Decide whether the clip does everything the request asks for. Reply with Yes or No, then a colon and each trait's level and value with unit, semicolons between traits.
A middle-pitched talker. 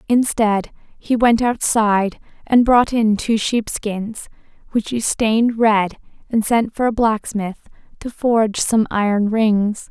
No: high, 220 Hz